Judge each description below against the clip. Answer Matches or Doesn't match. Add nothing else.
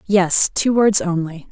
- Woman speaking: Matches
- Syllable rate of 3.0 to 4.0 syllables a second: Matches